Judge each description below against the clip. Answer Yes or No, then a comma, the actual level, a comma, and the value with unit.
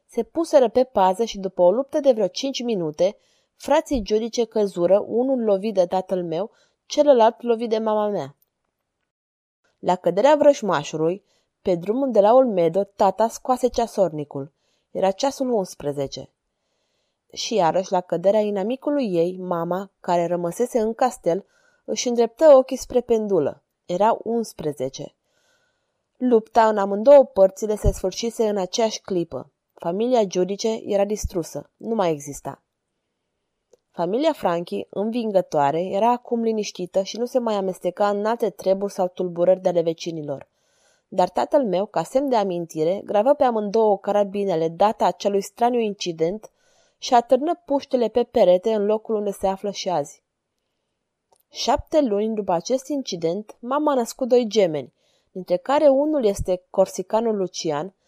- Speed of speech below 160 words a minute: Yes, average, 140 wpm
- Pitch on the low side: No, high, 205 Hz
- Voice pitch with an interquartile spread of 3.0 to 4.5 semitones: No, average, 5.0 semitones